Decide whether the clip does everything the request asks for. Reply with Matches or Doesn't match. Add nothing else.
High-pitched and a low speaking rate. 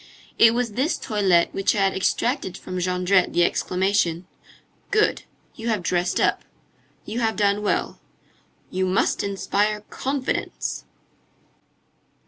Matches